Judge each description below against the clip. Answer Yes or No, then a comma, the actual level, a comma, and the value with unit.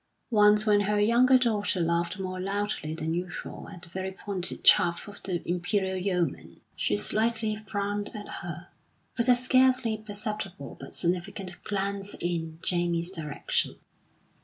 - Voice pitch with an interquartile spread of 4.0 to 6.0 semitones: No, average, 3.3 semitones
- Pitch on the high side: Yes, high, 195 Hz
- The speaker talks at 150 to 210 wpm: No, average, 140 wpm